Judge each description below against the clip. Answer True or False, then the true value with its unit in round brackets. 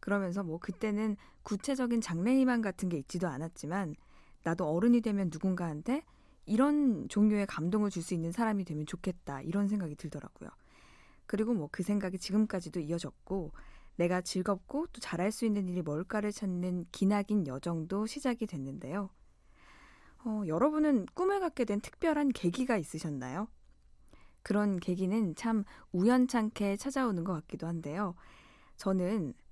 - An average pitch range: True (4.3 semitones)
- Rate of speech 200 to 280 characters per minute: False (325 characters per minute)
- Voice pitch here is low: False (195 Hz)